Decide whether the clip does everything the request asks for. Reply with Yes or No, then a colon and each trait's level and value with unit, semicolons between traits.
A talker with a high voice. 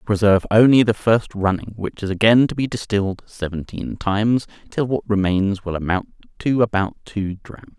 No: low, 105 Hz